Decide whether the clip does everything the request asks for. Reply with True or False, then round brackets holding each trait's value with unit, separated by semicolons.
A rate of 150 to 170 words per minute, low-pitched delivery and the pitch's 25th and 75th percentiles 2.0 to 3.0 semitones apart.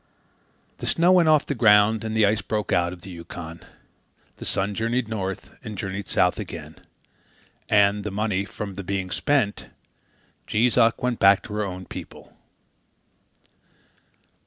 True (155 wpm; 105 Hz; 2.6 semitones)